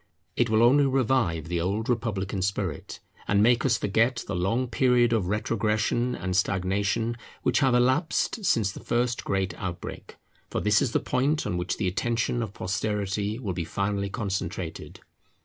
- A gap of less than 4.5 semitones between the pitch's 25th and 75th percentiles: Yes, average, 3.9 semitones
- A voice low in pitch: Yes, low, 105 Hz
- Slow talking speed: No, average, 165 wpm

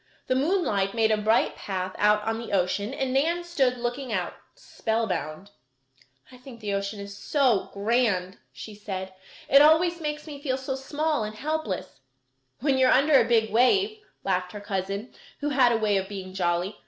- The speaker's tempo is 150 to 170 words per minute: No, average, 180 wpm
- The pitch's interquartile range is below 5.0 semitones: No, wide, 5.4 semitones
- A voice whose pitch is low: No, high, 225 Hz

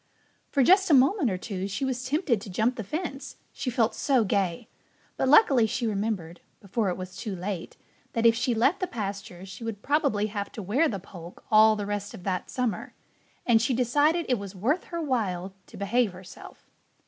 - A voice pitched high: Yes, high, 225 Hz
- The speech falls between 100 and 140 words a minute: No, average, 200 wpm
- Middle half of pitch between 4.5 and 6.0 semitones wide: Yes, average, 4.8 semitones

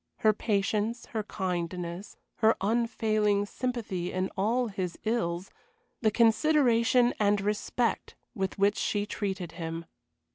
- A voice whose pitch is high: Yes, high, 210 Hz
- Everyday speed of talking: No, slow, 115 wpm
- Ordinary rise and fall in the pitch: Yes, average, 3.3 semitones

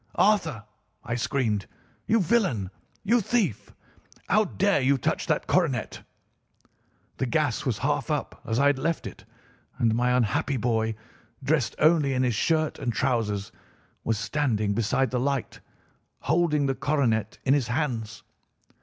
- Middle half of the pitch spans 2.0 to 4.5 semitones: No, average, 5.3 semitones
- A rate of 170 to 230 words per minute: No, average, 145 wpm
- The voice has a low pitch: Yes, low, 130 Hz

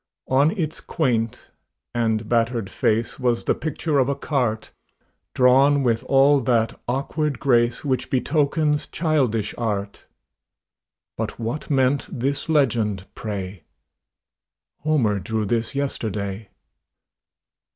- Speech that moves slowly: Yes, slow, 110 wpm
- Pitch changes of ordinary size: Yes, average, 4.1 semitones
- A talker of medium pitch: No, low, 125 Hz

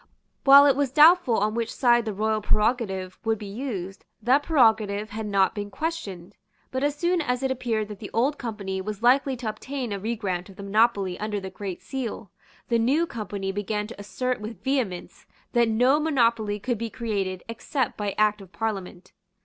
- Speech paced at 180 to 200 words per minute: Yes, average, 190 wpm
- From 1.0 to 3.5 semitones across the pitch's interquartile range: No, average, 3.9 semitones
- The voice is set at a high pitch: Yes, high, 220 Hz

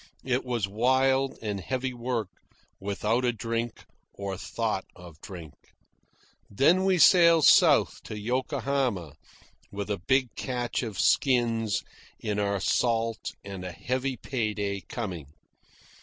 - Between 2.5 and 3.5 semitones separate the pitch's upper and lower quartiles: No, average, 4.4 semitones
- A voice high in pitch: No, low, 115 Hz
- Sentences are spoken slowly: Yes, slow, 125 wpm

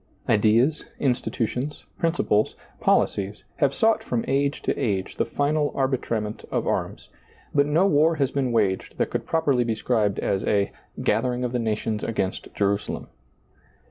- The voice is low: Yes, low, 125 Hz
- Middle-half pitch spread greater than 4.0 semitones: Yes, average, 5.1 semitones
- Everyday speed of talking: Yes, average, 150 wpm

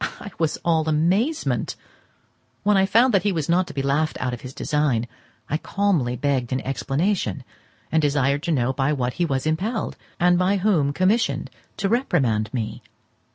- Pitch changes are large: Yes, wide, 6.2 semitones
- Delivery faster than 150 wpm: Yes, average, 175 wpm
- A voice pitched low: No, medium, 155 Hz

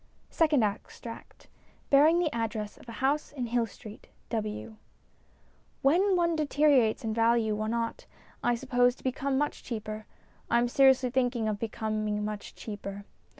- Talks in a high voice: Yes, high, 235 Hz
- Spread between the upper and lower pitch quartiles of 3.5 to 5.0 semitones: Yes, average, 4.0 semitones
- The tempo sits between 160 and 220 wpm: No, average, 150 wpm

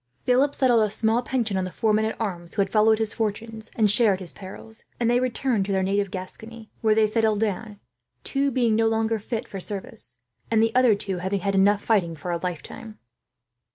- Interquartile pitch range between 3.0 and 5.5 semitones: No, narrow, 2.5 semitones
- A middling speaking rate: No, fast, 210 wpm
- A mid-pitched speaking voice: No, high, 215 Hz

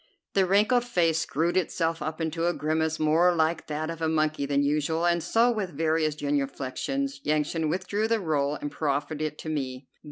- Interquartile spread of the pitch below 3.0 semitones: Yes, narrow, 2.5 semitones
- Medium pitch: Yes, medium, 160 Hz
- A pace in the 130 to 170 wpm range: No, average, 185 wpm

